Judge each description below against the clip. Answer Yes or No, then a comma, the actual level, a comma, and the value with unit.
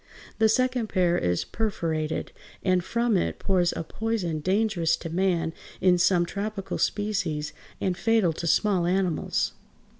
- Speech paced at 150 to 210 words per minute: No, average, 140 wpm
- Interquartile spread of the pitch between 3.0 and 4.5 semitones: Yes, average, 3.9 semitones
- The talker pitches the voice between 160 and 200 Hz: Yes, medium, 185 Hz